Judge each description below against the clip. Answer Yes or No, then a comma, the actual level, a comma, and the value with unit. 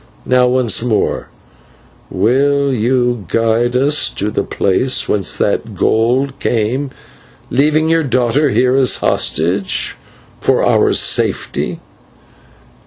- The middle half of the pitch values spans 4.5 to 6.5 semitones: No, average, 3.4 semitones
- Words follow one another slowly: Yes, slow, 105 wpm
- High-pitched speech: No, low, 125 Hz